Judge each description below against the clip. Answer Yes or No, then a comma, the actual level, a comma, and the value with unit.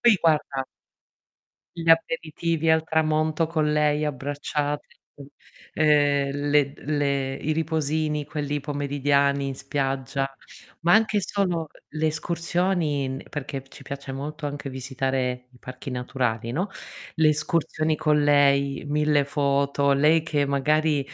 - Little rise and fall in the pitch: Yes, narrow, 2.1 semitones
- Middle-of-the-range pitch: Yes, medium, 145 Hz